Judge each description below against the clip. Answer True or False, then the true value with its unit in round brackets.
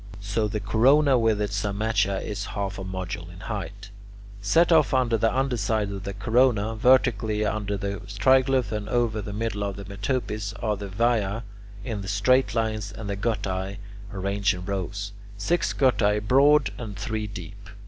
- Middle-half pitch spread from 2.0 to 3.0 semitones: True (2.5 semitones)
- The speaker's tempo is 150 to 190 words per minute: True (170 wpm)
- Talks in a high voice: False (105 Hz)